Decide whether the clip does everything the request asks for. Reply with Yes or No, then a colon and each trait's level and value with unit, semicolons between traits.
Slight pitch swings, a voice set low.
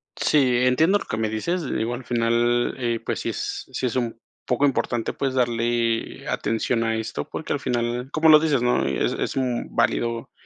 Yes: narrow, 2.1 semitones; low, 120 Hz